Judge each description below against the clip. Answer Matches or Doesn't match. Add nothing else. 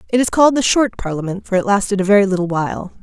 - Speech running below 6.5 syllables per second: Doesn't match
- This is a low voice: Doesn't match